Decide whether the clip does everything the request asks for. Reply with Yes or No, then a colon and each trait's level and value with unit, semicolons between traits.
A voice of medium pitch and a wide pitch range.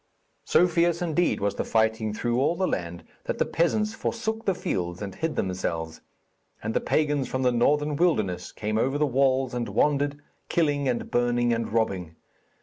No: low, 125 Hz; wide, 6.0 semitones